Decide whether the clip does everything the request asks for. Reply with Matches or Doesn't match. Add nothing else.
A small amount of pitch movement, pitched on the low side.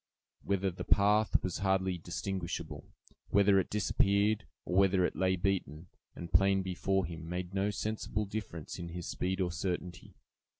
Matches